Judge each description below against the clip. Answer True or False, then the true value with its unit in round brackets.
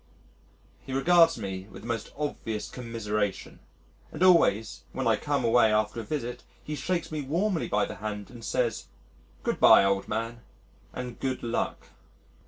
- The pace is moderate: True (160 wpm)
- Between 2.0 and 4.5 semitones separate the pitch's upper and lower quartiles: False (5.0 semitones)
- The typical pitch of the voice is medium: False (115 Hz)